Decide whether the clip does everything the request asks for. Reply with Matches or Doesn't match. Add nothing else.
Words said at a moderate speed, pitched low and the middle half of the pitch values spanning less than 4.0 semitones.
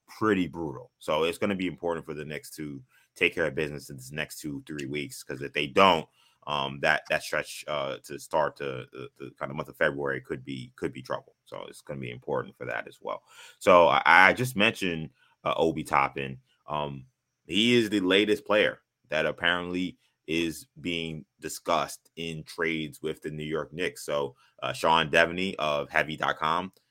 Matches